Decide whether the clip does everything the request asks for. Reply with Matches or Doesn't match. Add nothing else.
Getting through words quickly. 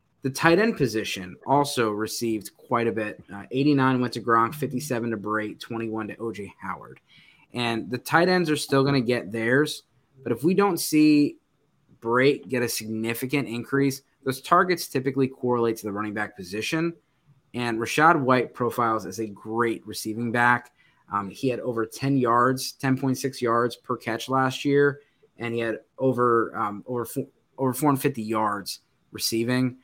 Doesn't match